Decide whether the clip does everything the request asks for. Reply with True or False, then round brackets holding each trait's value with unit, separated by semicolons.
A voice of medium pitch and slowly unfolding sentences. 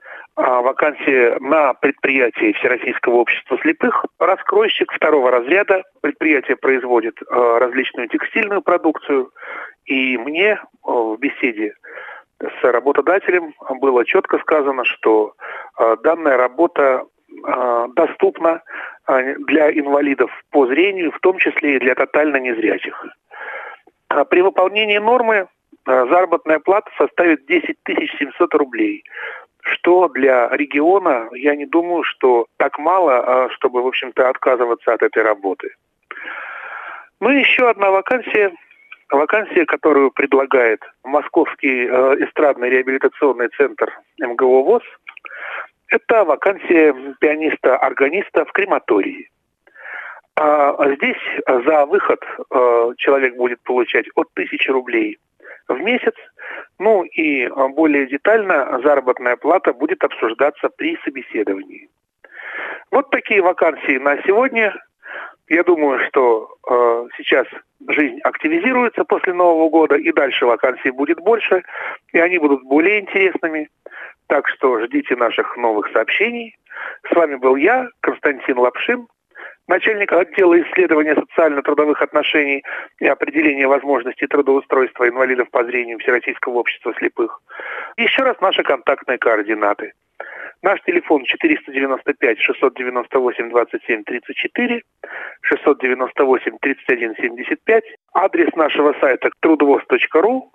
True (170 Hz; 100 wpm)